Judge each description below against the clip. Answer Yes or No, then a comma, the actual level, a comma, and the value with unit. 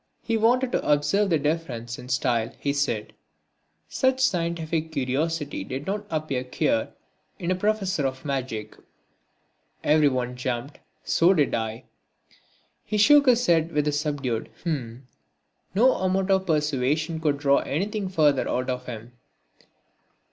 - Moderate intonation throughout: No, wide, 6.3 semitones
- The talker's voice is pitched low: No, medium, 150 Hz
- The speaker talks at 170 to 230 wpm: No, slow, 135 wpm